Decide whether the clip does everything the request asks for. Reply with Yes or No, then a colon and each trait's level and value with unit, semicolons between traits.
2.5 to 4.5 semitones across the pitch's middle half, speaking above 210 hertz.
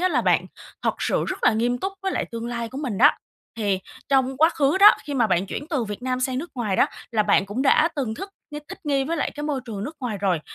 No: average, 4.9 semitones; very high, 255 Hz